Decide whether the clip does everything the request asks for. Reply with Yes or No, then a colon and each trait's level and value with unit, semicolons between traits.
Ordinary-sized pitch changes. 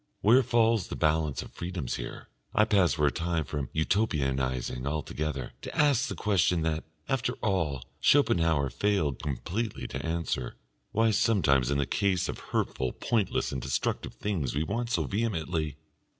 No: wide, 6.8 semitones